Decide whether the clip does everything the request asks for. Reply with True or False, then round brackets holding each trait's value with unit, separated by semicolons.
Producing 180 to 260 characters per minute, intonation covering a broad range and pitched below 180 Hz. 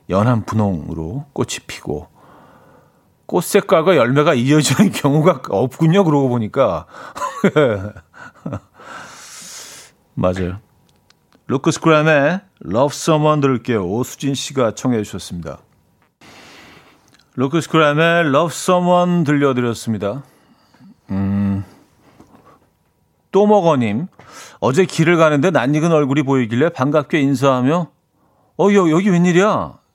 True (235 characters per minute; 6.0 semitones; 140 Hz)